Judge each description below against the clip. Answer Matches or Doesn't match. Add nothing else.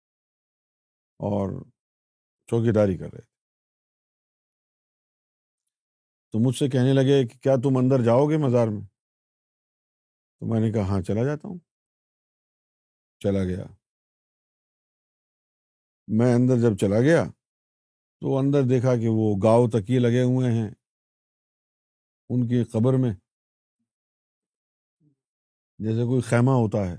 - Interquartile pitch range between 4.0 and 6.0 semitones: Matches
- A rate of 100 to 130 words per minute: Matches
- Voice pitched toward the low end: Matches